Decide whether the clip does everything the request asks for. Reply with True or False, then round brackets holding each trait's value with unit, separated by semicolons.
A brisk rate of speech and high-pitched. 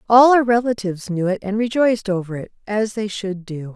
True (210 wpm; 210 Hz)